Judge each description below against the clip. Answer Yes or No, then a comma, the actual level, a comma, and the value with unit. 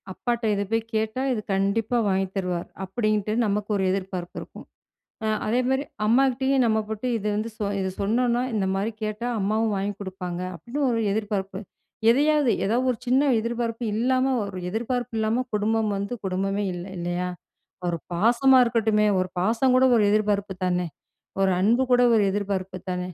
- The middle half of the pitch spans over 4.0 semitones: No, average, 3.7 semitones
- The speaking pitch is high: Yes, high, 215 Hz